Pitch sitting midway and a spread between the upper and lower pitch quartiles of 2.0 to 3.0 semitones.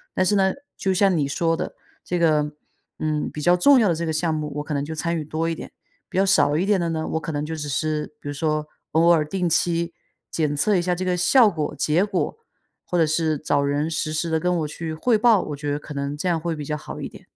Yes: medium, 160 Hz; average, 2.7 semitones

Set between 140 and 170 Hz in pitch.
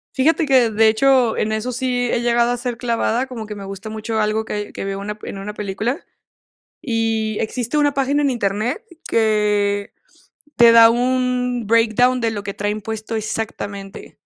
No: high, 225 Hz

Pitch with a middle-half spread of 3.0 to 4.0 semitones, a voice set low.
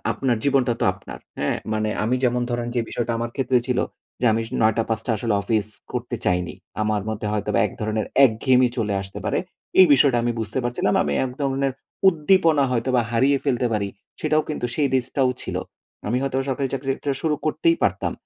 Yes: average, 3.6 semitones; low, 125 Hz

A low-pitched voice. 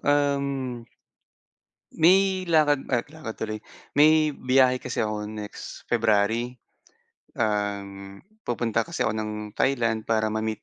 Yes: low, 115 Hz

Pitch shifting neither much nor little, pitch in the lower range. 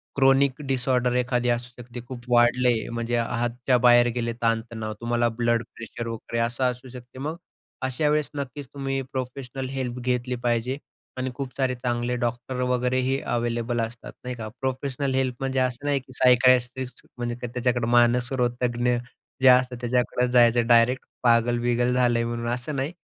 No: narrow, 1.4 semitones; low, 125 Hz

